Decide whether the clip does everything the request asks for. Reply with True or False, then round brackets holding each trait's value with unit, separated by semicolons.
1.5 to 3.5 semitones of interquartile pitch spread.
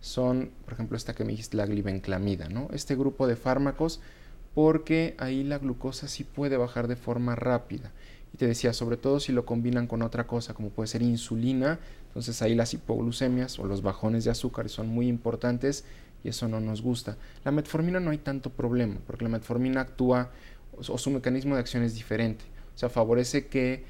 True (2.4 semitones)